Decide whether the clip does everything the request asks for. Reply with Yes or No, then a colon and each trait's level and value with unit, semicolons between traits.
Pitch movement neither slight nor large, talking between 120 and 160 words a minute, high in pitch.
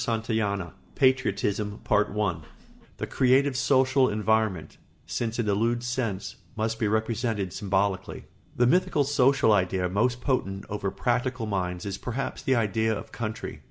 No: average, 3.7 semitones; slow, 135 wpm; low, 110 Hz